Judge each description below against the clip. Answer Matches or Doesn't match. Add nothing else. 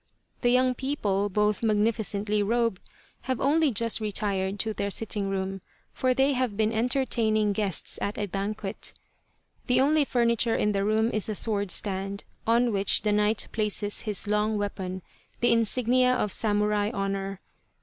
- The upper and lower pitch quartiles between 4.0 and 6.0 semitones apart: Doesn't match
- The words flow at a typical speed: Matches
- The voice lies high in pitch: Matches